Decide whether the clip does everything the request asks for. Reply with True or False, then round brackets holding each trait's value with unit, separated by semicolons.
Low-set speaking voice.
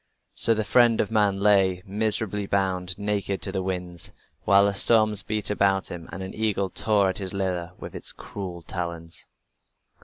True (100 Hz)